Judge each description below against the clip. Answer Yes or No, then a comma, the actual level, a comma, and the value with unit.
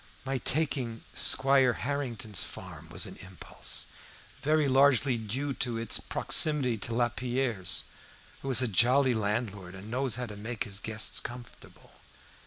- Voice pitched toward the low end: Yes, low, 120 Hz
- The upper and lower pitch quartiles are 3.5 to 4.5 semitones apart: Yes, average, 4.0 semitones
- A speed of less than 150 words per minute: Yes, average, 140 wpm